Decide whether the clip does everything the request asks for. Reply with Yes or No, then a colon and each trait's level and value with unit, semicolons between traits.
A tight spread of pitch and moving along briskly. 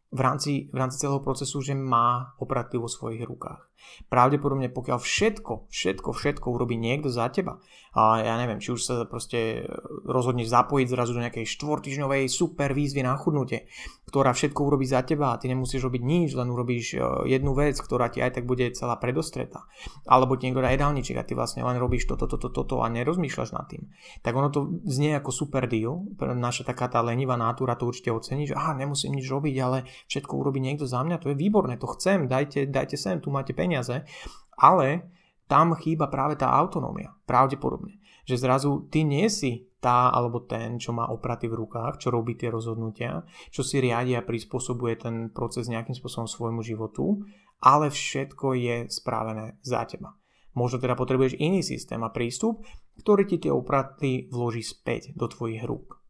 No: average, 3.0 semitones; fast, 180 wpm